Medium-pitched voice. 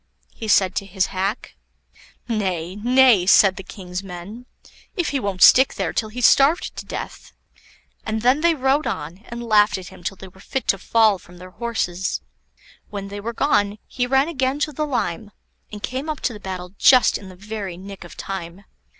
No: high, 205 Hz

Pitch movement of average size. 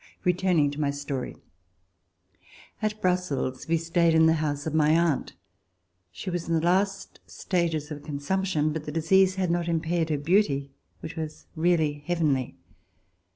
Yes: average, 3.0 semitones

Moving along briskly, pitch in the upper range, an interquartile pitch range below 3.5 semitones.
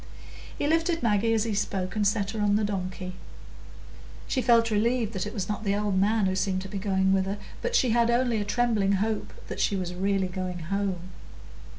Yes: fast, 215 wpm; high, 205 Hz; average, 3.0 semitones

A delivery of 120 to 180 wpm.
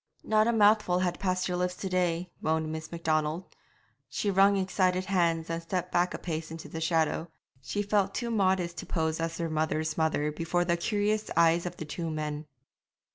No: average, 190 wpm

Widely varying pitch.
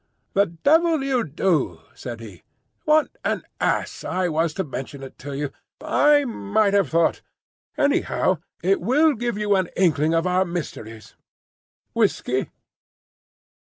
Yes: wide, 7.7 semitones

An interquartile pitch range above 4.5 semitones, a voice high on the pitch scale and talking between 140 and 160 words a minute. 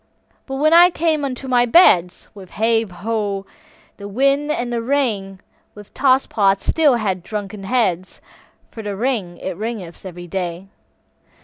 Yes: average, 5.2 semitones; high, 215 Hz; average, 150 wpm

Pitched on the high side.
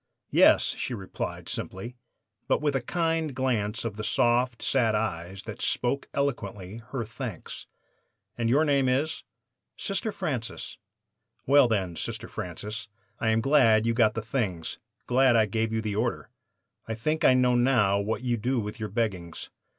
No: low, 115 Hz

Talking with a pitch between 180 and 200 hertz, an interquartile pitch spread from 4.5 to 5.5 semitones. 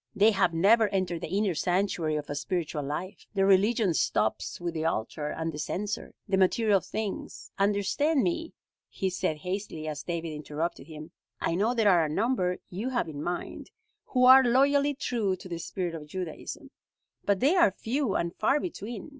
Yes: high, 190 Hz; average, 5.2 semitones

